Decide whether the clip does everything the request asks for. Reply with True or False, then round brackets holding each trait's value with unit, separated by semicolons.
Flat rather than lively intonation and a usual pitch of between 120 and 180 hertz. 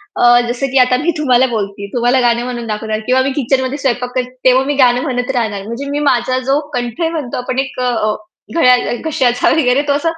False (1.8 semitones; 250 Hz)